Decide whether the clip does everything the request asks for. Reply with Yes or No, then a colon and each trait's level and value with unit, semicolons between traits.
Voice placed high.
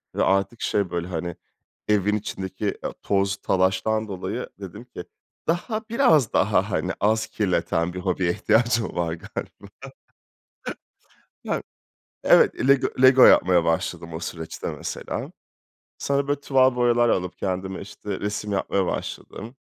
No: low, 100 Hz